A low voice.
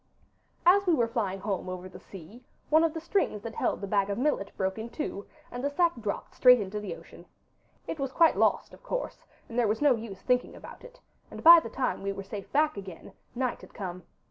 No: high, 230 Hz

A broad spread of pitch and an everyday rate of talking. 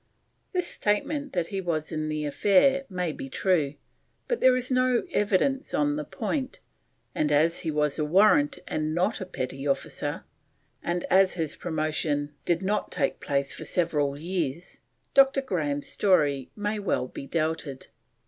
Yes: wide, 5.7 semitones; average, 155 wpm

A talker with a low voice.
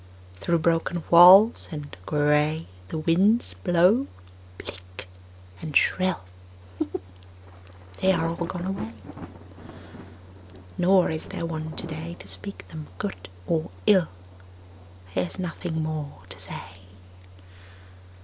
No: medium, 165 Hz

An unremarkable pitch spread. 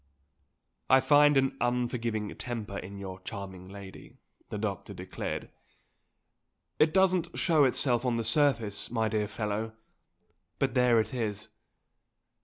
Yes: average, 4.1 semitones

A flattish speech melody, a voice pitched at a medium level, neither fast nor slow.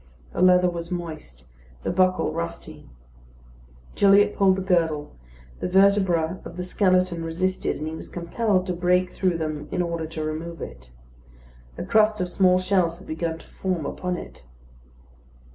Yes: narrow, 2.1 semitones; medium, 180 Hz; average, 160 wpm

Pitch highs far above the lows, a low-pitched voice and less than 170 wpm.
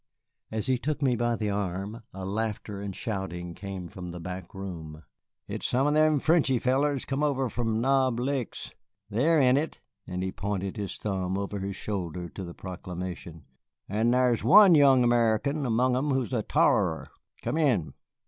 No: wide, 5.7 semitones; low, 110 Hz; average, 175 wpm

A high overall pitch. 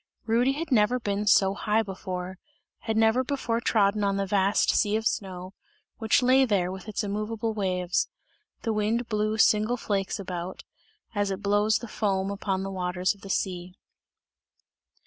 Yes: high, 205 Hz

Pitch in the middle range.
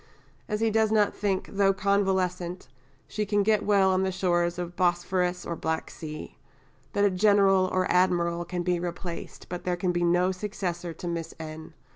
Yes: medium, 180 Hz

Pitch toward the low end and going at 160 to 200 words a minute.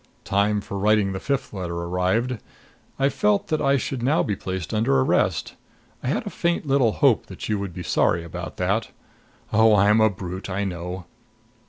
Yes: low, 100 Hz; average, 185 wpm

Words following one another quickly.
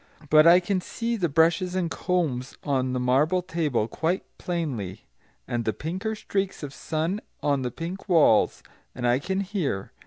No: average, 165 wpm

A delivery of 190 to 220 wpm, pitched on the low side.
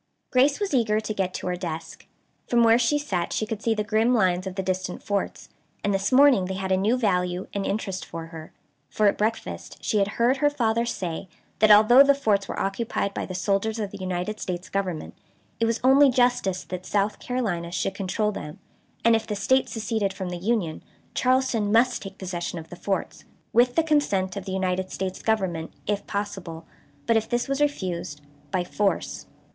No: average, 200 wpm; high, 205 Hz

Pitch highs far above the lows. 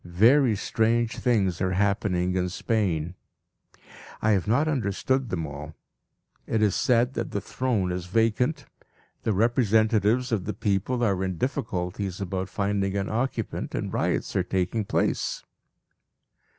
No: average, 3.9 semitones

